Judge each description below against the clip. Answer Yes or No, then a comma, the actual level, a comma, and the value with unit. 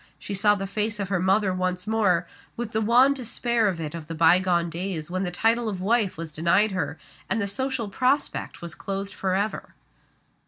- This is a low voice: No, high, 195 Hz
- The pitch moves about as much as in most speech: Yes, average, 3.6 semitones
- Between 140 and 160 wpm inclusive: No, average, 195 wpm